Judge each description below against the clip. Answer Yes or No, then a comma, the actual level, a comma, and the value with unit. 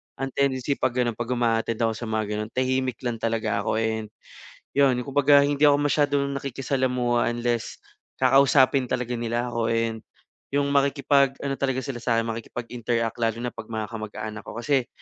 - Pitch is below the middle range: Yes, low, 120 Hz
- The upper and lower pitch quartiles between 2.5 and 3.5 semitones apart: Yes, average, 3.0 semitones